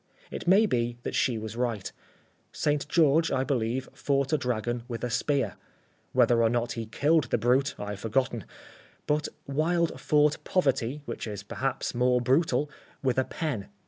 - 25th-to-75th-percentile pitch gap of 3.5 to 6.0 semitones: Yes, average, 4.0 semitones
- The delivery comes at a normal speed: Yes, average, 170 wpm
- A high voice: No, low, 130 Hz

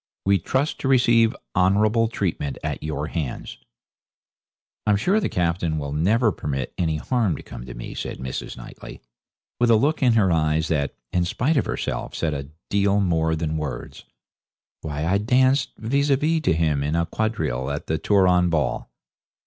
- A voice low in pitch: Yes, very low, 90 Hz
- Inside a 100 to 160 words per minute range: No, average, 175 wpm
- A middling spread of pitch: No, wide, 6.7 semitones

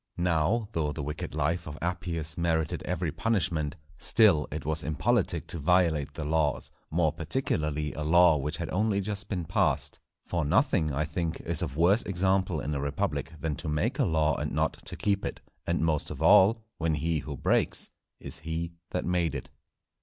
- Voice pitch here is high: No, very low, 80 Hz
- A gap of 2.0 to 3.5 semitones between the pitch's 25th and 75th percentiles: Yes, average, 2.8 semitones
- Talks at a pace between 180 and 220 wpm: Yes, average, 185 wpm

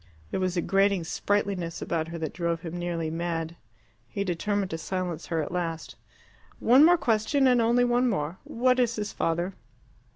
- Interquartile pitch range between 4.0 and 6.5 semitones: Yes, average, 5.0 semitones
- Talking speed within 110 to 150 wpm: No, average, 175 wpm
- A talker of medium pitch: Yes, medium, 180 Hz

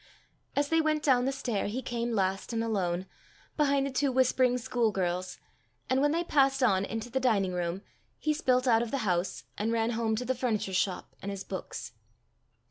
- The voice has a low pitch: No, high, 235 Hz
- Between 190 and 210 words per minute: Yes, average, 200 wpm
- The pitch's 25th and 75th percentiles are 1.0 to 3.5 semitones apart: No, average, 5.0 semitones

